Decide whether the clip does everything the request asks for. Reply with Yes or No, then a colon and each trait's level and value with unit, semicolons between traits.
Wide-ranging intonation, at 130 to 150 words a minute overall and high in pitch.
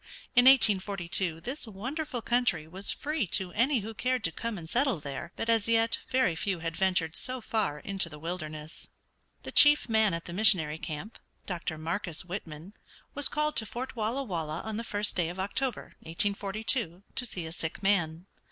No: wide, 5.7 semitones; average, 180 wpm; high, 200 Hz